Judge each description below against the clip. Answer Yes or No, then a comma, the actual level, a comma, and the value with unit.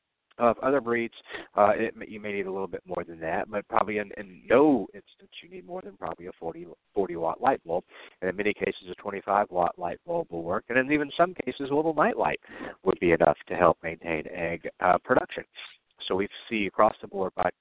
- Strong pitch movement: Yes, wide, 6.5 semitones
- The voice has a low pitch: Yes, low, 105 Hz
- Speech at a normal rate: No, fast, 225 wpm